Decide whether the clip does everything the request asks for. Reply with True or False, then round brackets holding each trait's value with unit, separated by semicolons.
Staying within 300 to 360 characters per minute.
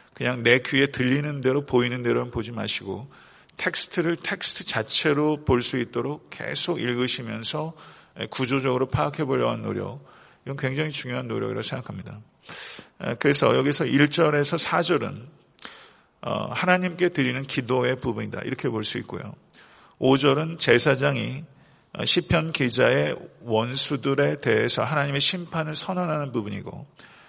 True (310 characters per minute)